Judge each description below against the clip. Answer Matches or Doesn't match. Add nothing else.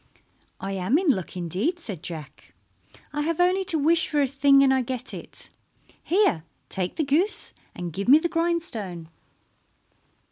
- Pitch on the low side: Doesn't match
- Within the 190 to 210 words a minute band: Doesn't match